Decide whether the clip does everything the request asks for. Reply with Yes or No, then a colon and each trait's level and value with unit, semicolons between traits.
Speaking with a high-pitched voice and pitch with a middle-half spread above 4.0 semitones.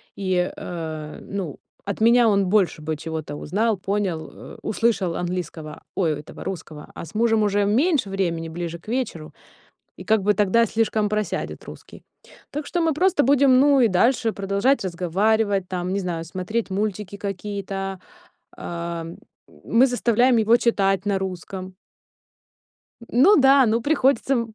Yes: high, 200 Hz; average, 4.5 semitones